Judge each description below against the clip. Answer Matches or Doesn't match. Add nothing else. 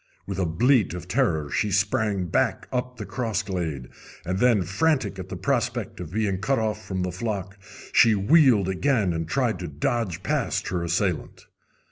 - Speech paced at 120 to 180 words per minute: Matches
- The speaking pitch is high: Doesn't match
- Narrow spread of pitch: Doesn't match